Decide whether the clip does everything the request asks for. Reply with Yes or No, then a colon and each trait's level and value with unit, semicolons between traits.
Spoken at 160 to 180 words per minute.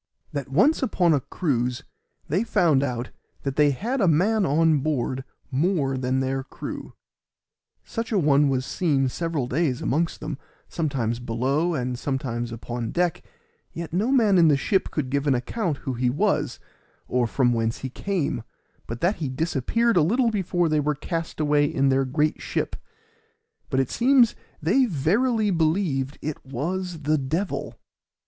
Yes: average, 165 wpm